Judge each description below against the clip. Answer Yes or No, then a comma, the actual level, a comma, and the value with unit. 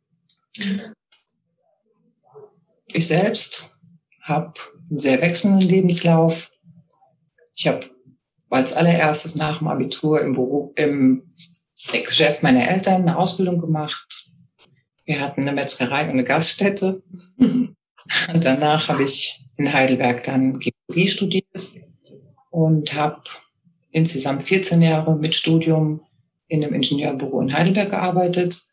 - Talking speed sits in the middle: No, slow, 110 wpm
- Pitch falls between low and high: Yes, medium, 160 Hz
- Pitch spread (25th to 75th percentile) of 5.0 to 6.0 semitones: No, average, 3.7 semitones